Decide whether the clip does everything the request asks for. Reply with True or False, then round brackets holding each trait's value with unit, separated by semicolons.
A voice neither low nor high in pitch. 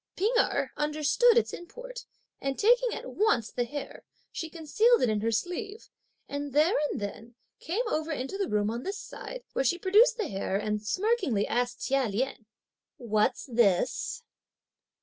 False (295 Hz)